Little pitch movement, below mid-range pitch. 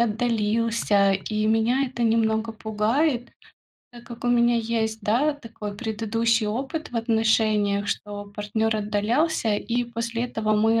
No: narrow, 1.8 semitones; high, 225 Hz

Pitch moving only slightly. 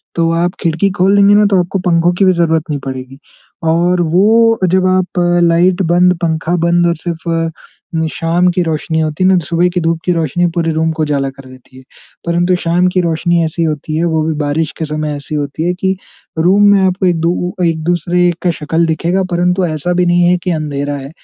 Yes: narrow, 2.1 semitones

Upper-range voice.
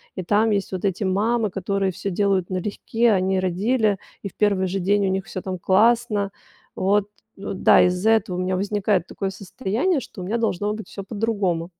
Yes: high, 195 Hz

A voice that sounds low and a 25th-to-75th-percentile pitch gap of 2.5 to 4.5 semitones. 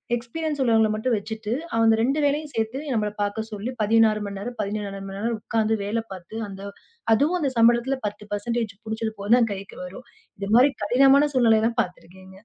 No: high, 225 Hz; average, 2.8 semitones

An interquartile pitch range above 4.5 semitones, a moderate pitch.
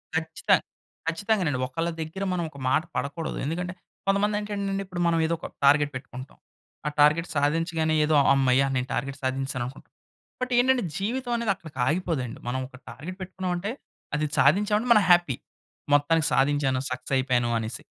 Yes: wide, 5.6 semitones; medium, 160 Hz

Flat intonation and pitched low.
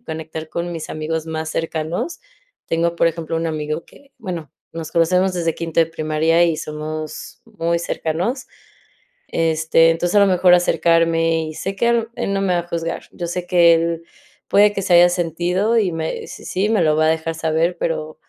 No: narrow, 1.9 semitones; medium, 165 Hz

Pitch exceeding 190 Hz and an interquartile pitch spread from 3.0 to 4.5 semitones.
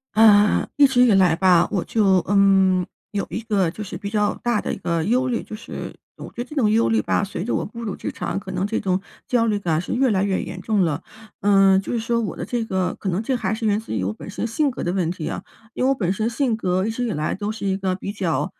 Yes: high, 205 Hz; average, 3.4 semitones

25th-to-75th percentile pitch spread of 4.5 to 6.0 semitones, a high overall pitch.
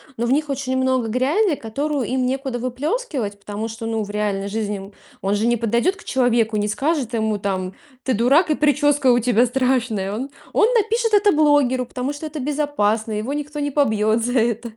Yes: average, 4.8 semitones; very high, 250 Hz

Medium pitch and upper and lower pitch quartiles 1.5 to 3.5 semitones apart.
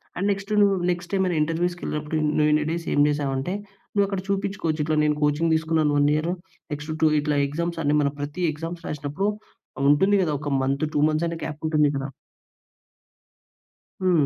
Yes: medium, 155 Hz; average, 3.0 semitones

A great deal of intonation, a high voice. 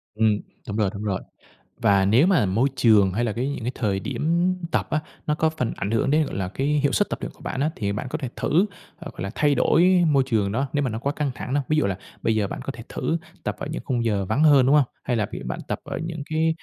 No: wide, 6.1 semitones; low, 130 Hz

